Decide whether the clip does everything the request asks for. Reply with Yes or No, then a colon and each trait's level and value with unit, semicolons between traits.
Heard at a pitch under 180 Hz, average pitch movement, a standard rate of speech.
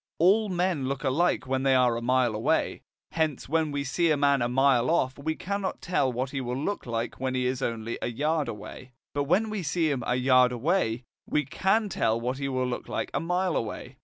No: low, 135 Hz; average, 4.5 semitones; fast, 225 wpm